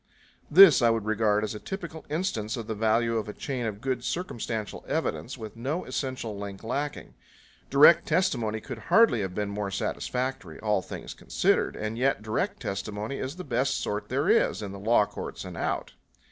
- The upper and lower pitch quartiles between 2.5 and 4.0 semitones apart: No, average, 4.4 semitones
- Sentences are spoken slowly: No, average, 185 wpm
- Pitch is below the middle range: Yes, low, 115 Hz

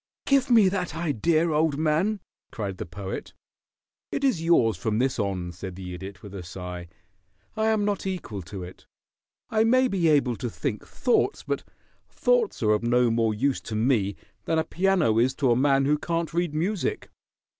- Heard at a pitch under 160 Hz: Yes, medium, 140 Hz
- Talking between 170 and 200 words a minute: Yes, average, 185 wpm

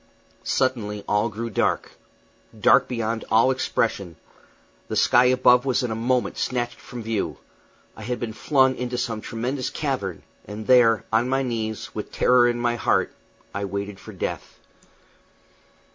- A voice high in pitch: No, low, 115 Hz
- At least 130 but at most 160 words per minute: Yes, average, 150 wpm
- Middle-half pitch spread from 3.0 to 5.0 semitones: No, narrow, 2.4 semitones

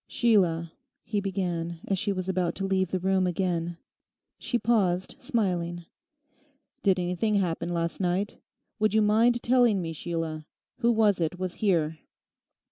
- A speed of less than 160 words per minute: Yes, average, 145 wpm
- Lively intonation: No, average, 3.4 semitones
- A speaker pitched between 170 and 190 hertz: Yes, medium, 185 Hz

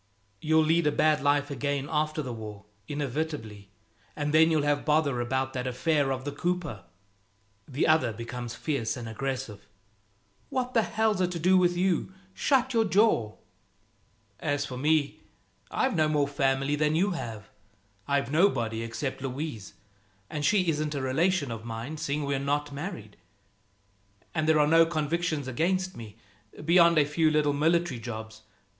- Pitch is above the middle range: No, medium, 145 Hz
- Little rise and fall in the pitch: No, average, 3.9 semitones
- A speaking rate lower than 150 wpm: No, average, 160 wpm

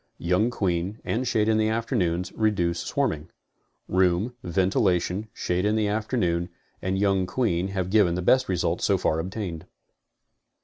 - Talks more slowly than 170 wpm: Yes, average, 145 wpm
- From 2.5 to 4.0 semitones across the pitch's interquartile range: Yes, average, 3.6 semitones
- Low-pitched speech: Yes, very low, 95 Hz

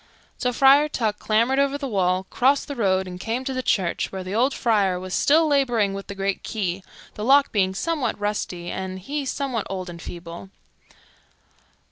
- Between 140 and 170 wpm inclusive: No, average, 185 wpm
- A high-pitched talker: Yes, high, 210 Hz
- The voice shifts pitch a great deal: Yes, wide, 6.1 semitones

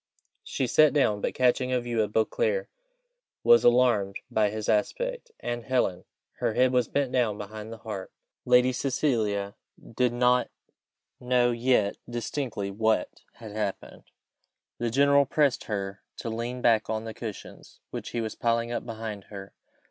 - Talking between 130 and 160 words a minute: Yes, average, 155 wpm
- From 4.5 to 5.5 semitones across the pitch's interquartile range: No, average, 2.8 semitones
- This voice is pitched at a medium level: No, low, 115 Hz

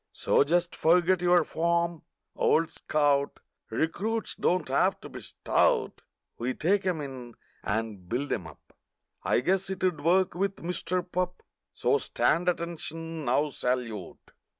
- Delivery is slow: Yes, slow, 130 wpm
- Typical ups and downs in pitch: Yes, average, 5.0 semitones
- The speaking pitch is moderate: Yes, medium, 165 Hz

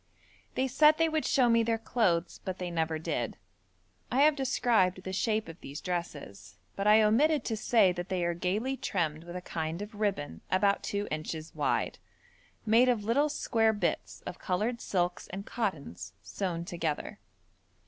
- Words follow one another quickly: No, average, 170 wpm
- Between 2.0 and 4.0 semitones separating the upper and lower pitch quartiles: No, average, 5.2 semitones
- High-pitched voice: Yes, high, 195 Hz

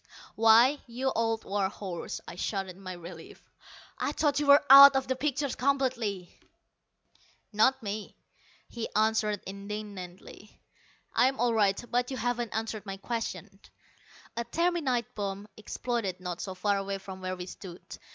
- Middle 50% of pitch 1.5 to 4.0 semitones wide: No, average, 4.4 semitones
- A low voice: No, high, 215 Hz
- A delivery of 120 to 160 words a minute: Yes, average, 150 wpm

